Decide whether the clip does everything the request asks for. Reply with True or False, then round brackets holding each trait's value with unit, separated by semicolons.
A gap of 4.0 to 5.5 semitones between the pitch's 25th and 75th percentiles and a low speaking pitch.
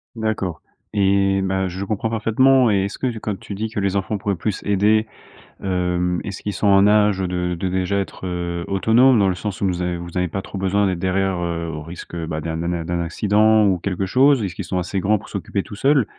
False (2.8 semitones; 95 Hz)